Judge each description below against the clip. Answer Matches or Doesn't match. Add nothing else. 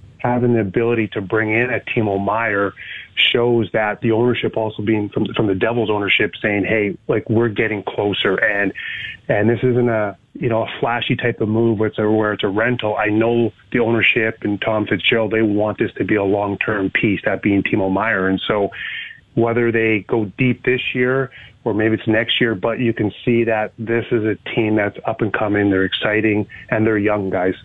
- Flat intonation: Matches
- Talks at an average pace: Doesn't match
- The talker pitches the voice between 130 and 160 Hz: Doesn't match